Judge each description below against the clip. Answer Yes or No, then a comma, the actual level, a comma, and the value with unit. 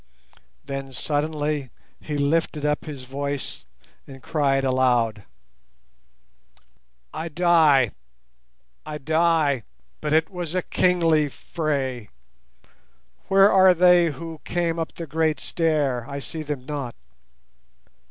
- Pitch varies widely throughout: No, average, 3.2 semitones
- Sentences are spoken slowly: Yes, slow, 105 wpm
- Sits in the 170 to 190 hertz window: No, medium, 150 Hz